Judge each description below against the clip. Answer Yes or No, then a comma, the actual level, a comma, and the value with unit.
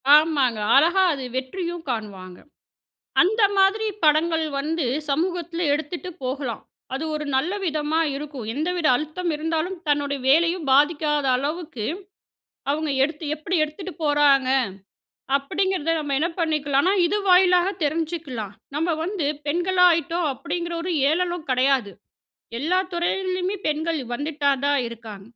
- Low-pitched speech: No, very high, 310 Hz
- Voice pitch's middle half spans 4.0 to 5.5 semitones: No, average, 3.6 semitones